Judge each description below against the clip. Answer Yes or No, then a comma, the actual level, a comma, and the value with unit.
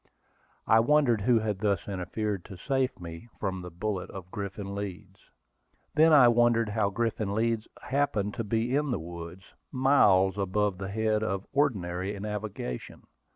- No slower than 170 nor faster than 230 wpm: No, average, 155 wpm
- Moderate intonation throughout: Yes, average, 3.4 semitones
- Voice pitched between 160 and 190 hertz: No, low, 105 Hz